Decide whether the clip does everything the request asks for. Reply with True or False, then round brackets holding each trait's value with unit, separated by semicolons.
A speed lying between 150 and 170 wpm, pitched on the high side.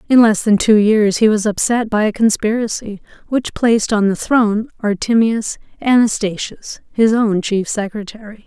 True (155 wpm; 215 Hz)